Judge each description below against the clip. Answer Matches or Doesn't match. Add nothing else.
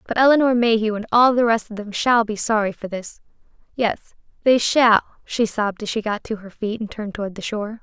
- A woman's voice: Matches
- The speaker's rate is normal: Doesn't match